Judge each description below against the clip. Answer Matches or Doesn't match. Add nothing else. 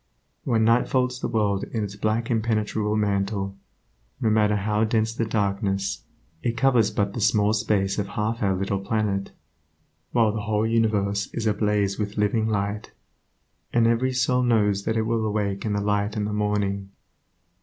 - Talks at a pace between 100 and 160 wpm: Doesn't match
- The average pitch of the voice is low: Matches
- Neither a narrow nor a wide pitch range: Doesn't match